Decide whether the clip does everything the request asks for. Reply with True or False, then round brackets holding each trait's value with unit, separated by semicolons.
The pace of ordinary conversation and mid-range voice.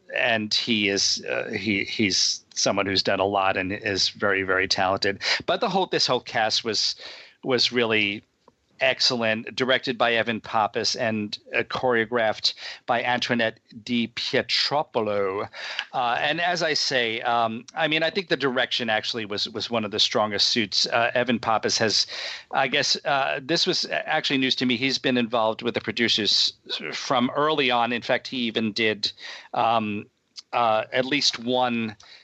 False (165 wpm; 115 Hz)